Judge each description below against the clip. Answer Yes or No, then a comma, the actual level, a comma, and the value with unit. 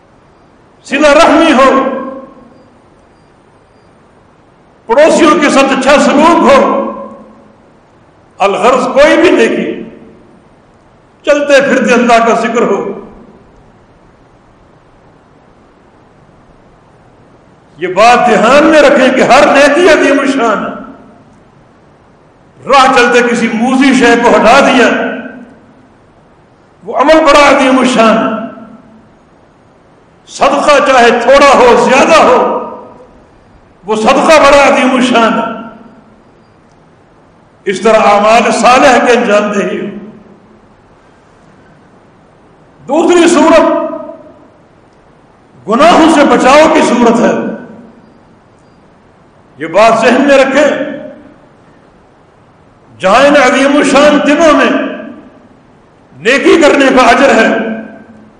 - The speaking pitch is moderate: No, very high, 265 Hz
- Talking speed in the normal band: No, slow, 85 wpm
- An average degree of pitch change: Yes, average, 3.9 semitones